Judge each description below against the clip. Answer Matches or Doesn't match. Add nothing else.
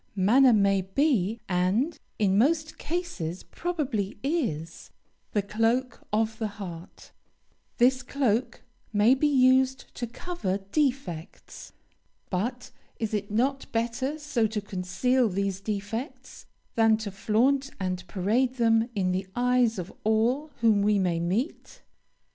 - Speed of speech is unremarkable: Doesn't match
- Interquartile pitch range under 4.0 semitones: Doesn't match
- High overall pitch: Matches